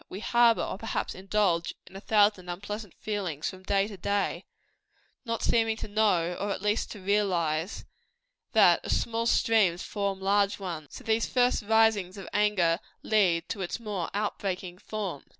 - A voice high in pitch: Yes, high, 200 Hz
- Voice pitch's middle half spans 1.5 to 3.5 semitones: Yes, average, 2.8 semitones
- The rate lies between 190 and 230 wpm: No, average, 165 wpm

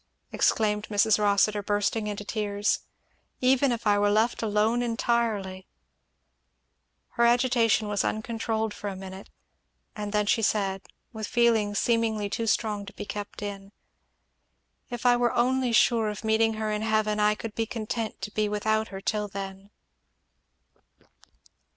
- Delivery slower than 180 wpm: Yes, average, 150 wpm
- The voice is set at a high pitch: Yes, high, 215 Hz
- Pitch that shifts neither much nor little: No, narrow, 1.7 semitones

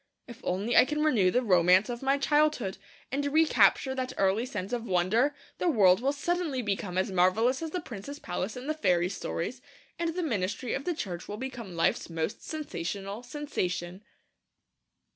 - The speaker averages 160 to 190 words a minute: Yes, average, 175 wpm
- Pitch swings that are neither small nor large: No, wide, 7.1 semitones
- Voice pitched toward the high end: Yes, high, 235 Hz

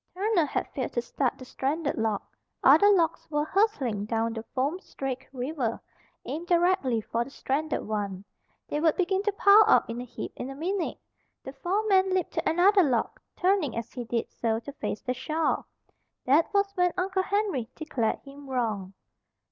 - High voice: Yes, very high, 290 Hz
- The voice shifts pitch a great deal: Yes, wide, 7.4 semitones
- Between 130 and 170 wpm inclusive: No, average, 180 wpm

